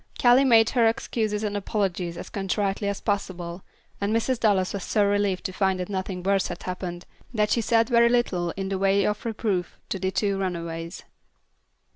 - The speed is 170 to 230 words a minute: Yes, average, 185 wpm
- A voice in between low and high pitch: No, high, 200 Hz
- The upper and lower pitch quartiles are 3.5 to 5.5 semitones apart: No, average, 2.8 semitones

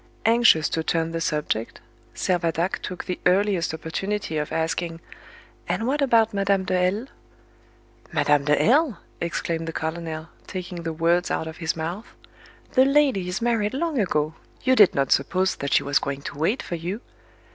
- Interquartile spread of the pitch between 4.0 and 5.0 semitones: Yes, average, 4.4 semitones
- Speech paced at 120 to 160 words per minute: No, average, 175 wpm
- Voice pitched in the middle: Yes, medium, 175 Hz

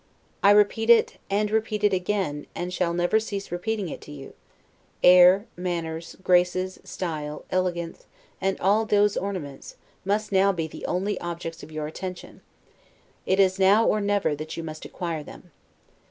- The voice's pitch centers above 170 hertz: Yes, medium, 185 Hz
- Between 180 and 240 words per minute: No, average, 160 wpm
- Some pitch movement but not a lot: Yes, average, 3.3 semitones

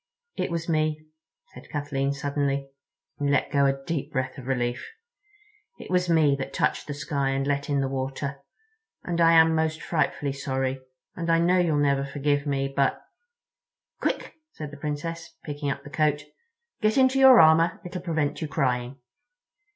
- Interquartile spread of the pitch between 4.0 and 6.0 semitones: No, average, 2.9 semitones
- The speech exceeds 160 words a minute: Yes, average, 170 wpm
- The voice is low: No, medium, 145 Hz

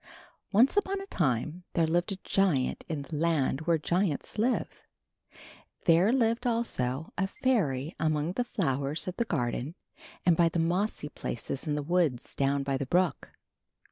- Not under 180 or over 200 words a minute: No, average, 160 wpm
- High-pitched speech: No, medium, 165 Hz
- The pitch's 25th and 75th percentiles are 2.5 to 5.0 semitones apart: No, wide, 5.6 semitones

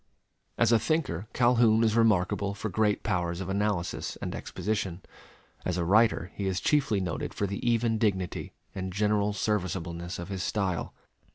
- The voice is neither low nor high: No, low, 100 Hz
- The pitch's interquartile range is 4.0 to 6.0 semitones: No, average, 3.1 semitones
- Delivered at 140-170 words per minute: Yes, average, 160 wpm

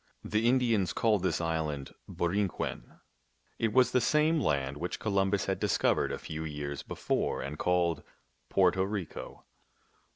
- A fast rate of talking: No, average, 140 wpm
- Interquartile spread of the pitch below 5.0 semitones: No, wide, 5.5 semitones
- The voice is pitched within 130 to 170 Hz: No, very low, 90 Hz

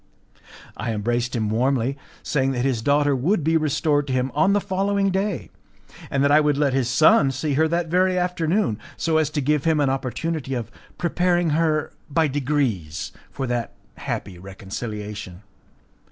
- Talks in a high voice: No, medium, 145 Hz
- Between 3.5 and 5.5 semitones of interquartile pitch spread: Yes, average, 4.9 semitones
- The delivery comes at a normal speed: Yes, average, 170 wpm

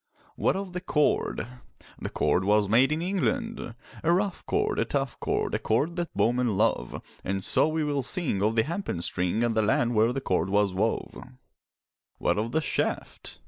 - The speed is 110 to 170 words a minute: No, average, 185 wpm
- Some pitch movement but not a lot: No, wide, 7.9 semitones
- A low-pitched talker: Yes, low, 120 Hz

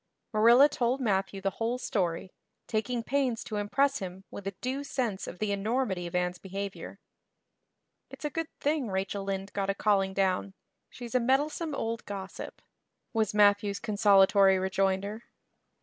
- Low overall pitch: No, high, 205 Hz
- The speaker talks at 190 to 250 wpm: No, average, 150 wpm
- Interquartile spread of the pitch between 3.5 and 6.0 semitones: Yes, average, 4.0 semitones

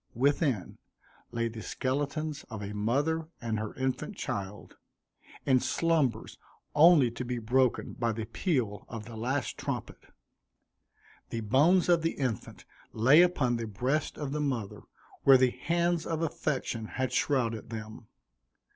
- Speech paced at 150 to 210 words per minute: No, average, 140 wpm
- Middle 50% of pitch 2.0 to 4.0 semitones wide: No, average, 4.8 semitones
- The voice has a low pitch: Yes, low, 130 Hz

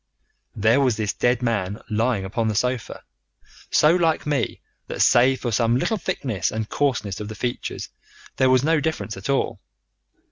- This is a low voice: Yes, low, 120 Hz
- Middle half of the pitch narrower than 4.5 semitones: Yes, average, 4.1 semitones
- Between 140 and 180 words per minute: Yes, average, 170 wpm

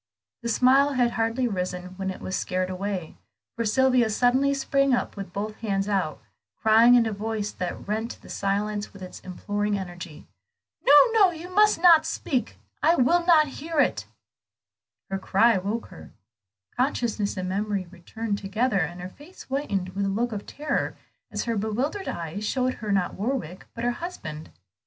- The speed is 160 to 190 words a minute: Yes, average, 175 wpm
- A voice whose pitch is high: Yes, high, 215 Hz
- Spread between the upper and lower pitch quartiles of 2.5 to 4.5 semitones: No, average, 5.0 semitones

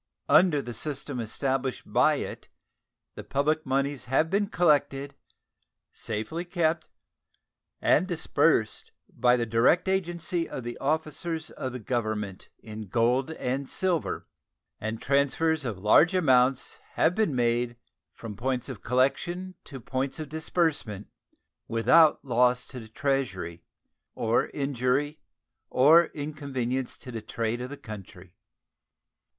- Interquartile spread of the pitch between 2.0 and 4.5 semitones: No, average, 4.9 semitones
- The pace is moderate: No, slow, 120 wpm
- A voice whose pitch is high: No, low, 135 Hz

